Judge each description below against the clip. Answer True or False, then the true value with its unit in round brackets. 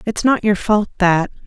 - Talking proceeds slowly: False (205 wpm)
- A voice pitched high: True (200 Hz)